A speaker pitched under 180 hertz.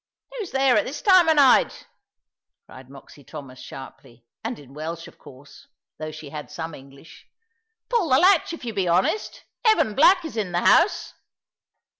No: medium, 185 Hz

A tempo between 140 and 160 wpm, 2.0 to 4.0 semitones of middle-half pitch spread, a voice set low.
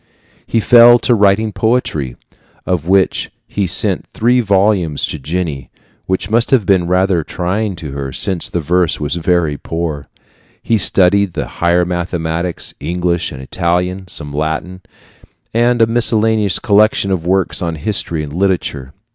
Yes: average, 145 wpm; average, 3.7 semitones; very low, 90 Hz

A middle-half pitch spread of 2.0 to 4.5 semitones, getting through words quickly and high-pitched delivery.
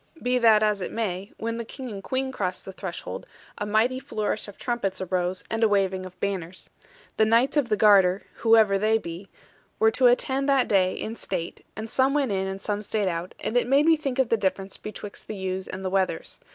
Yes: average, 3.7 semitones; fast, 220 wpm; high, 210 Hz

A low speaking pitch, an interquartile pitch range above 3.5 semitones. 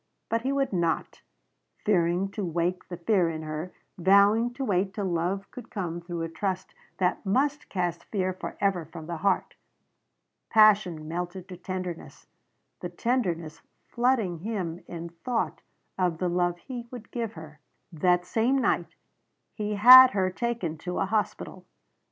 No: medium, 185 Hz; average, 4.1 semitones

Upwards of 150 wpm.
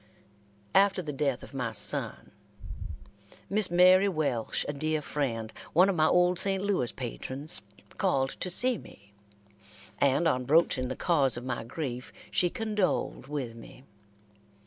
No: average, 145 wpm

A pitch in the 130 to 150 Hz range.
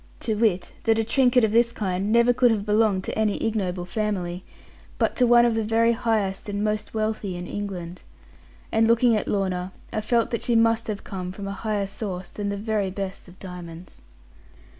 No: high, 210 Hz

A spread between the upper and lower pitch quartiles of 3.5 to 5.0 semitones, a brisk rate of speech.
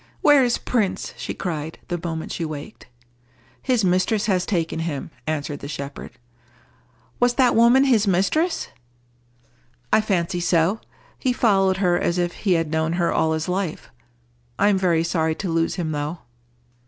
No: average, 4.7 semitones; average, 160 wpm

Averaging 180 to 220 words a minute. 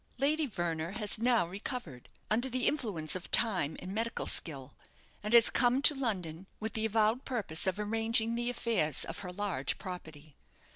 No: average, 165 wpm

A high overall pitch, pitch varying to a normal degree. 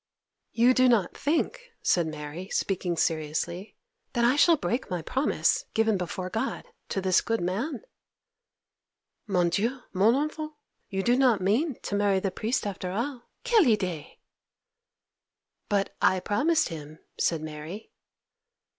No: high, 205 Hz; wide, 6.1 semitones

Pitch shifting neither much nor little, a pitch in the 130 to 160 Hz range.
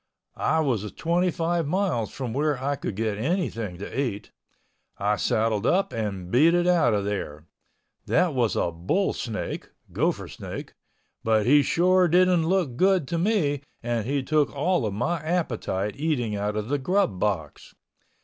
No: wide, 8.1 semitones; low, 135 Hz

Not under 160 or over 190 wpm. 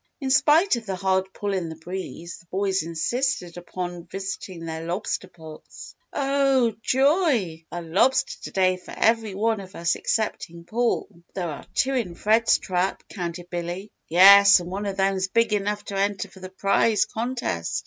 Yes: average, 175 wpm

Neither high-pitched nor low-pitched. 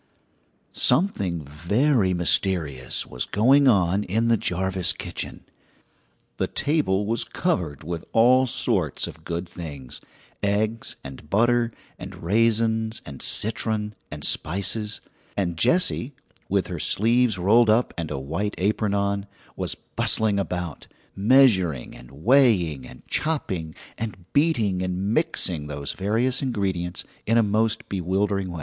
No: low, 100 Hz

